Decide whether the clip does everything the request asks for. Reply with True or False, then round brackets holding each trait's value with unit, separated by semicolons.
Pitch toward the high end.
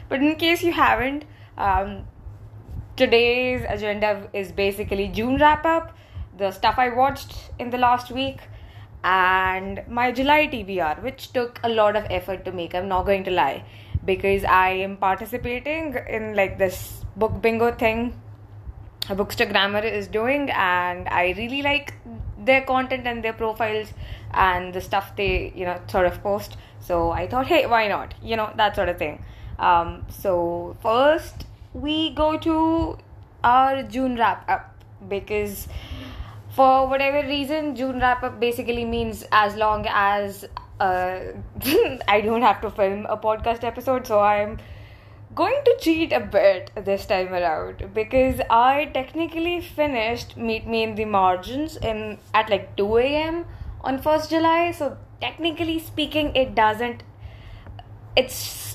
True (215 Hz)